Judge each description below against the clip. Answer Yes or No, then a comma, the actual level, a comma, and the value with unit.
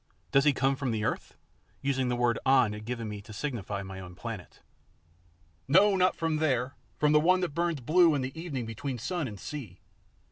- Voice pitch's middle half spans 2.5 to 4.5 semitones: No, average, 5.2 semitones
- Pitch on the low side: Yes, low, 130 Hz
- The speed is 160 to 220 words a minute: Yes, average, 200 wpm